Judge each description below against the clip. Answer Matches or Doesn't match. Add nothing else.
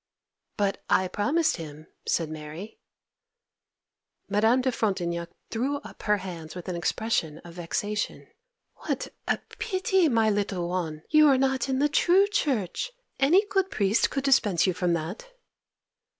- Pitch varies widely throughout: Matches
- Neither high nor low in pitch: Doesn't match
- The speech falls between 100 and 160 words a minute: Matches